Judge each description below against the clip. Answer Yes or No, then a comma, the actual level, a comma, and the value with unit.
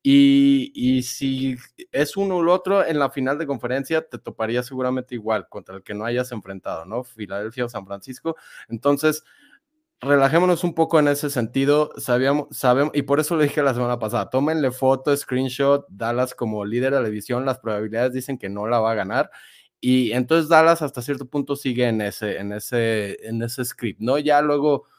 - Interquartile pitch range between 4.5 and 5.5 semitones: No, average, 3.8 semitones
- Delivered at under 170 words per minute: No, fast, 190 wpm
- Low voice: Yes, low, 130 Hz